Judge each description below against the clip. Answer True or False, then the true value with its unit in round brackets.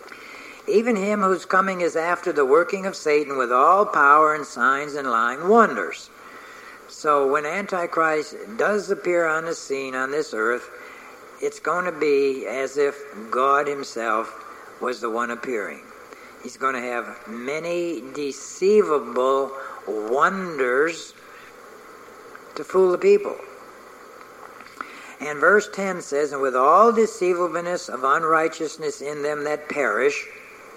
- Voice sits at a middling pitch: True (165 Hz)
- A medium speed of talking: False (130 wpm)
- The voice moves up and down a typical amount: False (7.3 semitones)